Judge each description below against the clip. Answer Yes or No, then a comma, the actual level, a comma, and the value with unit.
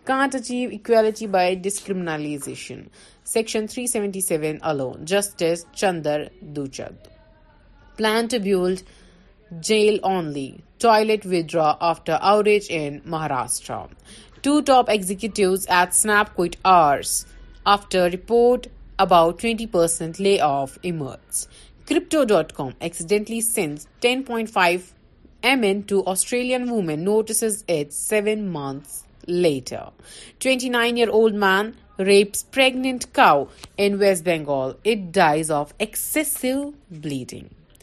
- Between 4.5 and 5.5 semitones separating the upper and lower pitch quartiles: Yes, average, 5.2 semitones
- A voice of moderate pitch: No, high, 195 Hz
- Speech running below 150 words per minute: Yes, average, 115 wpm